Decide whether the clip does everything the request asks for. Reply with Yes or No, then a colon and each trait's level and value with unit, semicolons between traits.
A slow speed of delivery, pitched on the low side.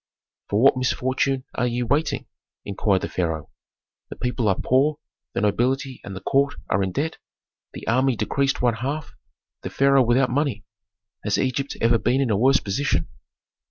No: average, 165 wpm; low, 125 Hz